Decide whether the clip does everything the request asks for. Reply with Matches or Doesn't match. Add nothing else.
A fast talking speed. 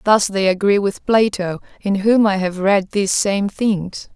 Doesn't match